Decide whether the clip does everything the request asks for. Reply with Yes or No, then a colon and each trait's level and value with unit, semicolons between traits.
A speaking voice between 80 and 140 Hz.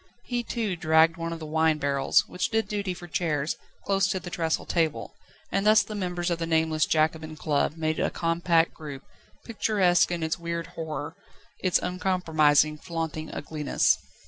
No: medium, 165 Hz